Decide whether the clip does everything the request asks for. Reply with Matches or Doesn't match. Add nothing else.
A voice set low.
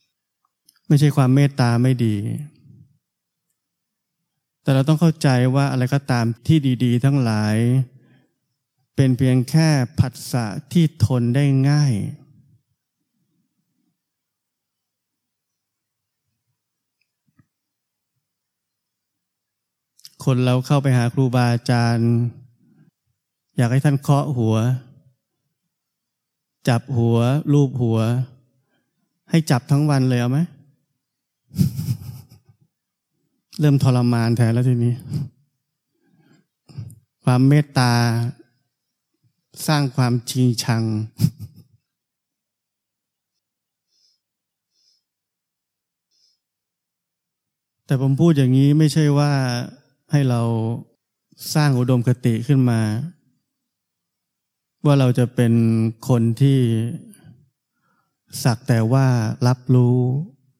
Matches